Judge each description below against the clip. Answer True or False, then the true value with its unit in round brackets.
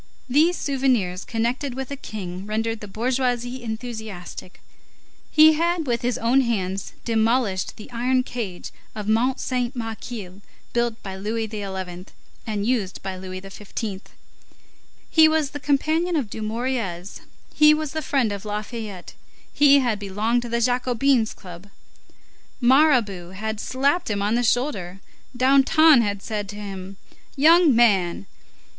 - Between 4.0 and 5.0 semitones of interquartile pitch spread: True (4.5 semitones)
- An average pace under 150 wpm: True (140 wpm)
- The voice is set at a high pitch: True (230 Hz)